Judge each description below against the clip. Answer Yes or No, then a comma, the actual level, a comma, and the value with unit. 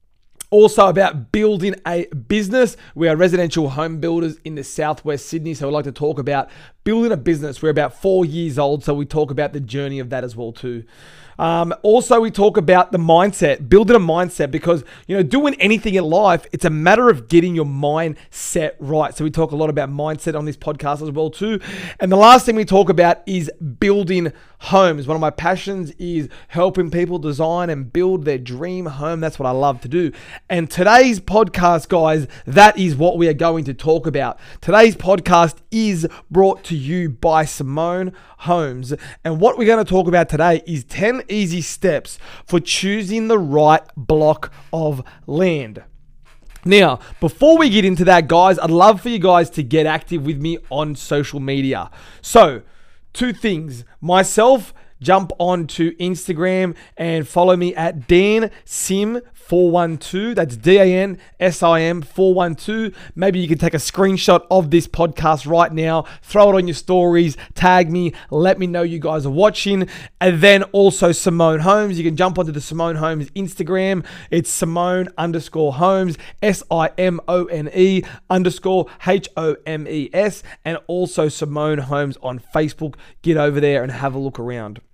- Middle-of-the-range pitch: Yes, medium, 170 Hz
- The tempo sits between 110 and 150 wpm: No, average, 170 wpm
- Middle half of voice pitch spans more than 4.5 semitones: No, average, 3.4 semitones